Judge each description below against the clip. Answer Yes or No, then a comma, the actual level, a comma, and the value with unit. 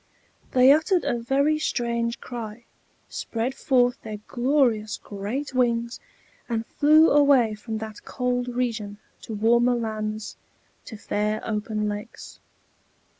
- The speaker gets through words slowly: Yes, slow, 120 wpm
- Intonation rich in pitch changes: No, average, 2.7 semitones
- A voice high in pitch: Yes, high, 235 Hz